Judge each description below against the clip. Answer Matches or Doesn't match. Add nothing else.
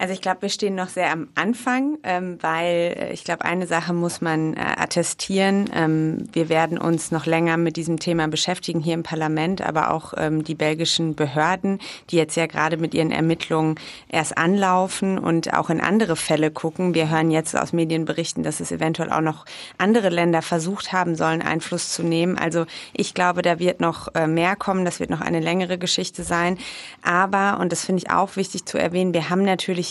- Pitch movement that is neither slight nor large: Doesn't match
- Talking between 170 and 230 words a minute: Matches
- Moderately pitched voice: Matches